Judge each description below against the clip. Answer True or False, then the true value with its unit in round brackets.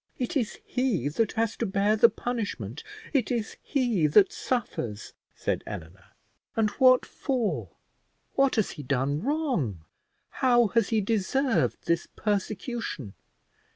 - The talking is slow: True (130 wpm)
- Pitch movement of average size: False (7.9 semitones)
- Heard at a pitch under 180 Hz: False (220 Hz)